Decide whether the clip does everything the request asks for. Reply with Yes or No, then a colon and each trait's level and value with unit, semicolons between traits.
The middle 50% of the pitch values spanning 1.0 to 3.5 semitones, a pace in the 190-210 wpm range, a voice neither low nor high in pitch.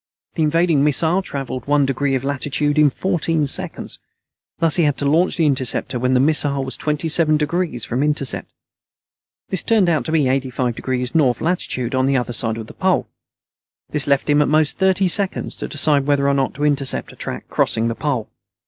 Yes: average, 3.2 semitones; average, 195 wpm; medium, 145 Hz